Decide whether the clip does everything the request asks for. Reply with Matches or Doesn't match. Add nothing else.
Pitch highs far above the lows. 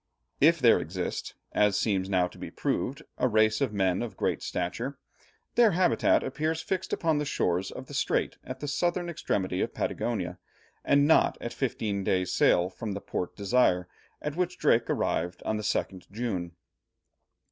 Matches